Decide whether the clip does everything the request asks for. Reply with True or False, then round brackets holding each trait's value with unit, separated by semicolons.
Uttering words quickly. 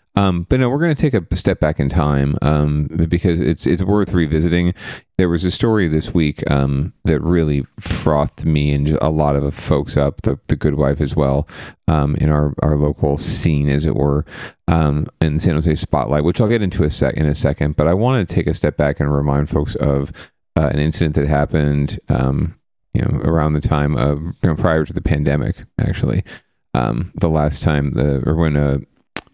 True (215 wpm)